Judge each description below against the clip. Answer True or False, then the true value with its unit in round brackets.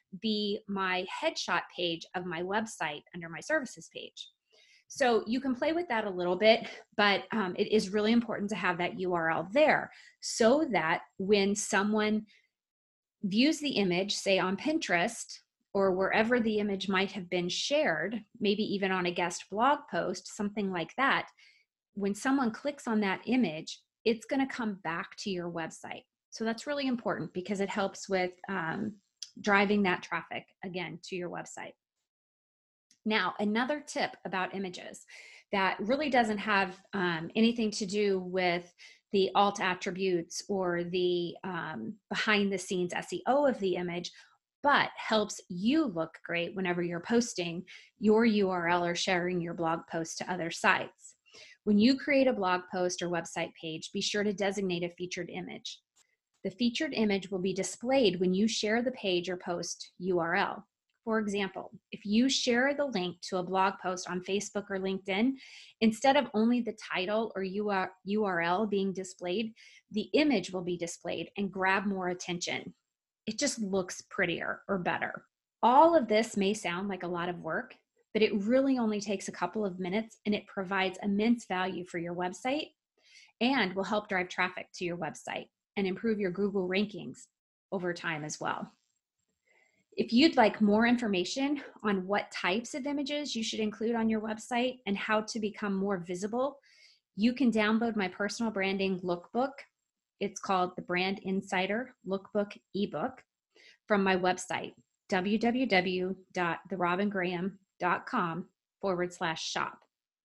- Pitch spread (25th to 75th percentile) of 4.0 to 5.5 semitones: False (3.3 semitones)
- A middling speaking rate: True (160 wpm)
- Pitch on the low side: False (200 Hz)